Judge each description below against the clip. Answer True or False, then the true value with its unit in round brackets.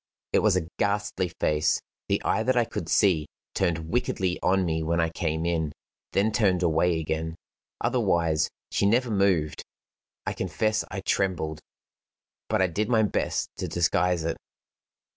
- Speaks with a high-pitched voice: False (90 Hz)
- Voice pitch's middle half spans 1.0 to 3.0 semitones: False (3.7 semitones)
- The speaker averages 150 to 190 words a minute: True (155 wpm)